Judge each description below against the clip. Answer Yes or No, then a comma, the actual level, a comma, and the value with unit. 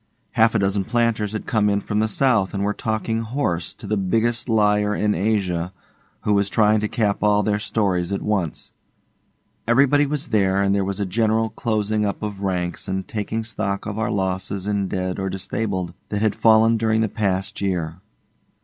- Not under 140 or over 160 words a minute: No, average, 190 wpm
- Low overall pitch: Yes, low, 105 Hz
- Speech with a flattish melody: Yes, narrow, 2.3 semitones